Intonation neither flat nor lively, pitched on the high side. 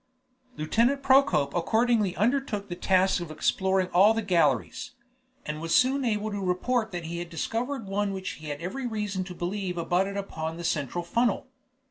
Yes: average, 4.7 semitones; high, 195 Hz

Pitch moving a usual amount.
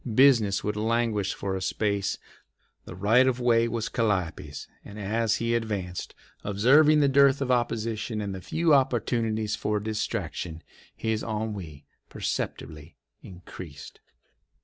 Yes: average, 3.1 semitones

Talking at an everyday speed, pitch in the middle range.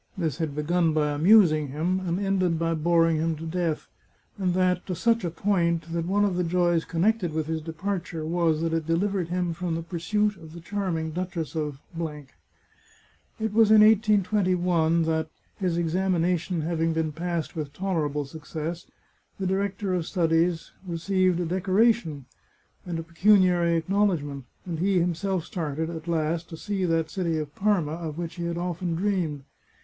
Yes: average, 170 wpm; medium, 170 Hz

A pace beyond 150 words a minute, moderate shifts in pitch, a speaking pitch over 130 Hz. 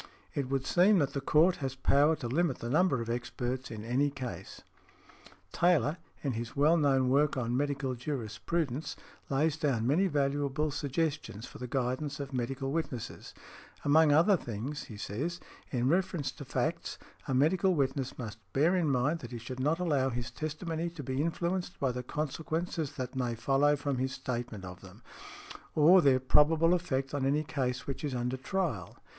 Yes: average, 175 wpm; average, 3.7 semitones; medium, 140 Hz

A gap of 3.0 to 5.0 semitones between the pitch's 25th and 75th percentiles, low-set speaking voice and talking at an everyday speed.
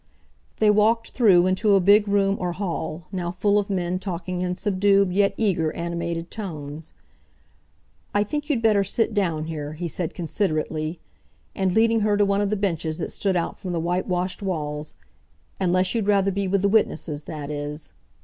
No: average, 3.3 semitones; medium, 185 Hz; average, 175 wpm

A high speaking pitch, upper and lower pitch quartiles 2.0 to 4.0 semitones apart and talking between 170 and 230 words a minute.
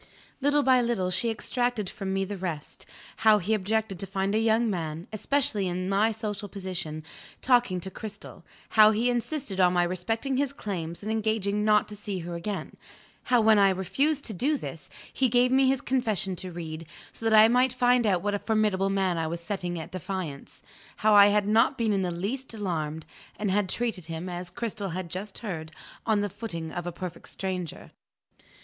Yes: high, 205 Hz; average, 3.6 semitones; average, 195 wpm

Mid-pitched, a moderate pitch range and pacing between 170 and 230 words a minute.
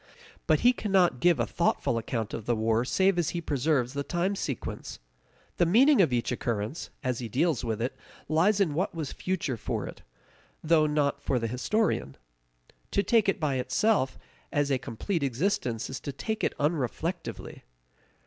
No: medium, 145 Hz; wide, 6.7 semitones; average, 175 wpm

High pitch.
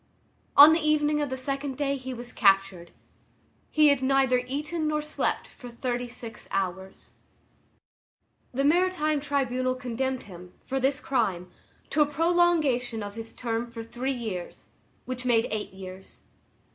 Yes: very high, 255 Hz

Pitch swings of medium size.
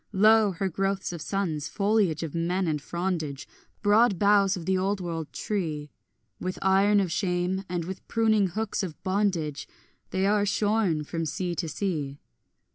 Yes: average, 3.5 semitones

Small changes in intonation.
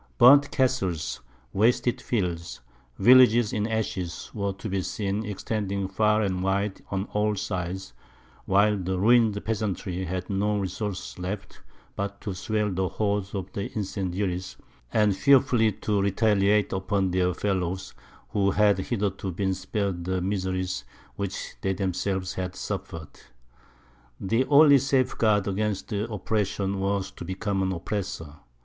Yes: narrow, 2.2 semitones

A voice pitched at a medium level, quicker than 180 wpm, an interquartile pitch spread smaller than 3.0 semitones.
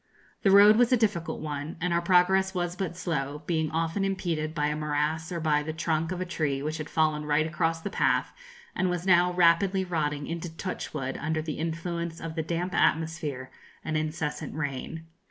Yes: medium, 165 Hz; average, 190 wpm; narrow, 2.6 semitones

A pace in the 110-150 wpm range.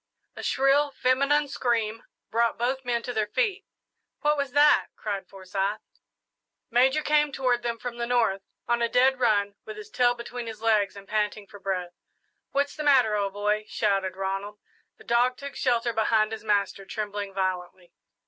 No: average, 170 wpm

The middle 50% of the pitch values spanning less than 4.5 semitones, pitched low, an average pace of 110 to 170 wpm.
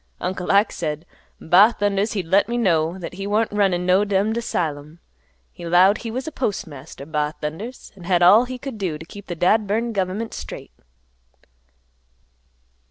No: average, 3.9 semitones; high, 190 Hz; average, 165 wpm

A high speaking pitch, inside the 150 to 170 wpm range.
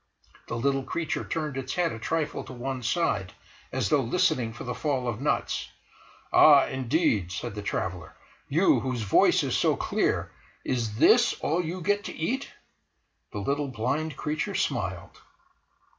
No: low, 135 Hz; average, 160 wpm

